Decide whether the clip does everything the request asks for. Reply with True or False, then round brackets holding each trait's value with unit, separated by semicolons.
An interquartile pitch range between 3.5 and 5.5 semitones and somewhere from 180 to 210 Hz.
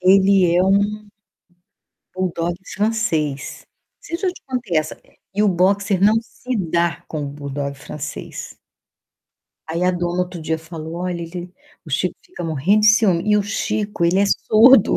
True (3.9 semitones; 185 Hz)